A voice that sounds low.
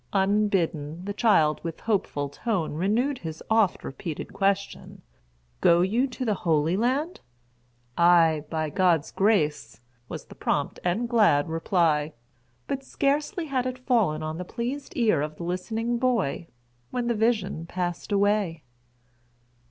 No: high, 190 Hz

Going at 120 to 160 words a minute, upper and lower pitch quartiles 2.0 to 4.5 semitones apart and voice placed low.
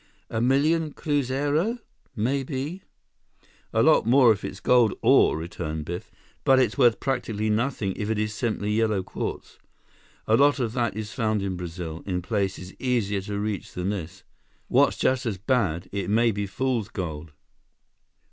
No: average, 155 wpm; average, 5.1 semitones; low, 110 Hz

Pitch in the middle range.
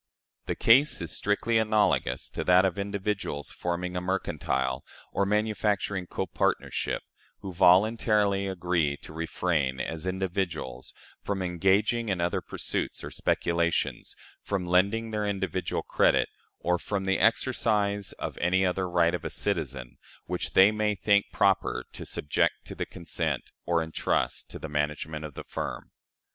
No: very low, 95 Hz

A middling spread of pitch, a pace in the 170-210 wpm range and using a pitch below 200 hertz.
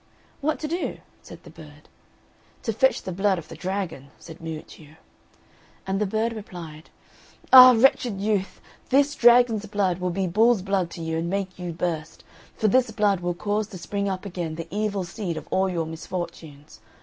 Yes: average, 4.1 semitones; average, 180 wpm; high, 190 Hz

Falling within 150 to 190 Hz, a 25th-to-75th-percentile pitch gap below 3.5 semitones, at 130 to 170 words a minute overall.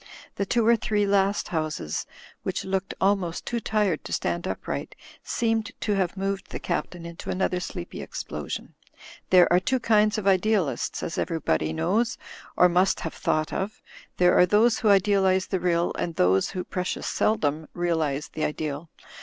No: medium, 185 Hz; average, 3.8 semitones; average, 165 wpm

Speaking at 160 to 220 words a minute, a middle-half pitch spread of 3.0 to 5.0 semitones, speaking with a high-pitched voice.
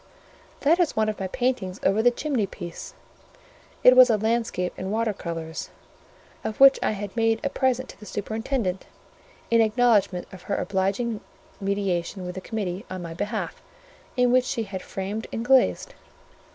Yes: average, 165 wpm; average, 4.2 semitones; high, 215 Hz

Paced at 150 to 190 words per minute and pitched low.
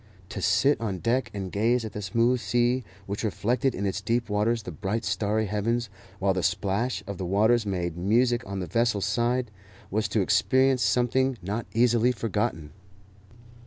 Yes: average, 170 wpm; low, 110 Hz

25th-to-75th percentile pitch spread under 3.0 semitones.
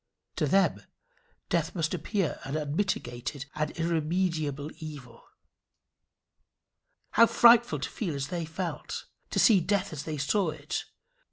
No: average, 4.4 semitones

